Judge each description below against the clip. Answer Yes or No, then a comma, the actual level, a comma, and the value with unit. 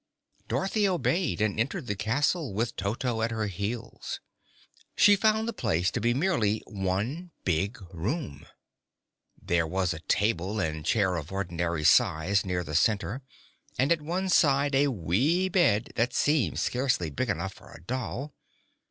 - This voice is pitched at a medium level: No, low, 110 Hz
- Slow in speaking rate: No, average, 150 wpm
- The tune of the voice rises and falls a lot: Yes, wide, 7.6 semitones